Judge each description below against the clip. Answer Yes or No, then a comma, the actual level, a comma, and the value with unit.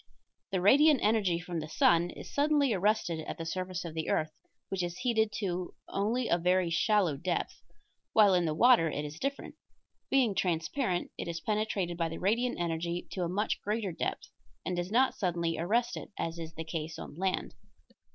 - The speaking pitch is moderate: Yes, medium, 180 Hz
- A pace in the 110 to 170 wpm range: No, average, 190 wpm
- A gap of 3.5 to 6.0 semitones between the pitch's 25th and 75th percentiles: Yes, average, 4.4 semitones